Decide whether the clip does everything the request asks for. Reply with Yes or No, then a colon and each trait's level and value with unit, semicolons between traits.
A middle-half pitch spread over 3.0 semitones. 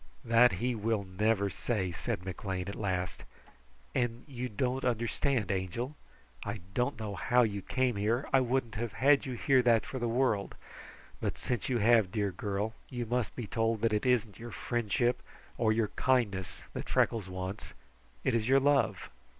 Yes: average, 3.4 semitones